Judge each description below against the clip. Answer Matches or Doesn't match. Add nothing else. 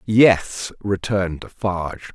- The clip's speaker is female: Doesn't match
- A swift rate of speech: Doesn't match